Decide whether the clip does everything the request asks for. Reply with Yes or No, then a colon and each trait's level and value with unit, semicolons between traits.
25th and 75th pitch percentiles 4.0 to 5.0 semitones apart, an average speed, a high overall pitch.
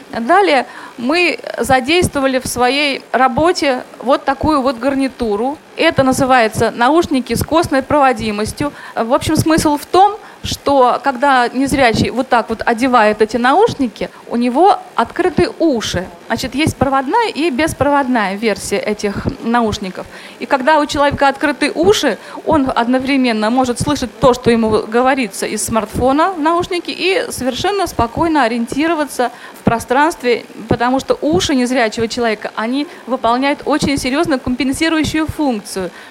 Yes: average, 4.3 semitones; average, 130 wpm; very high, 265 Hz